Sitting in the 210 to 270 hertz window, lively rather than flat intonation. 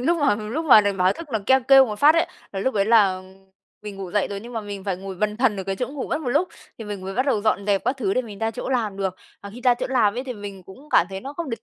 No: high, 215 Hz; average, 4.7 semitones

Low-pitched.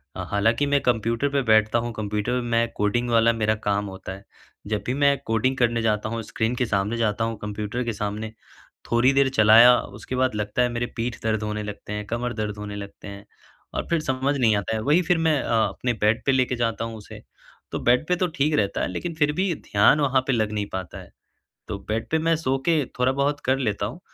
Yes: low, 115 Hz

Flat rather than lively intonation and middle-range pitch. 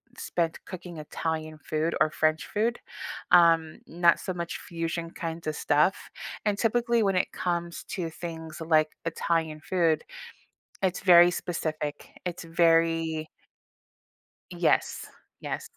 Yes: narrow, 1.7 semitones; medium, 165 Hz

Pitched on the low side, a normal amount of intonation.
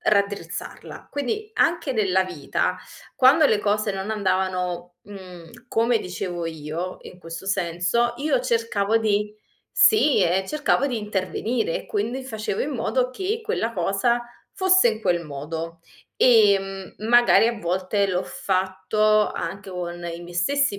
No: high, 200 Hz; average, 4.8 semitones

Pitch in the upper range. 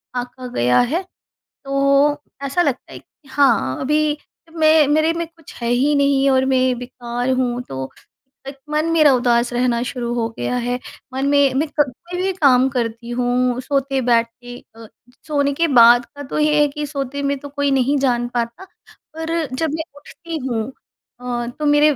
Yes: very high, 270 Hz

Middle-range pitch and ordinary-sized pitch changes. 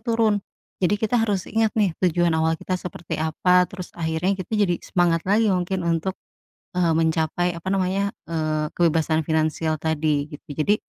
Yes: medium, 175 Hz; average, 3.4 semitones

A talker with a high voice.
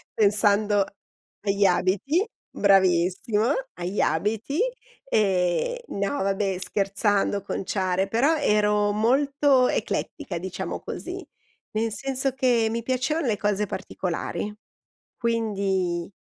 Yes: high, 205 Hz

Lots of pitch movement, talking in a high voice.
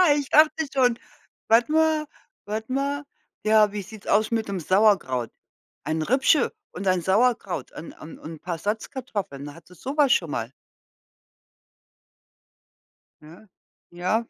Yes: wide, 6.9 semitones; high, 215 Hz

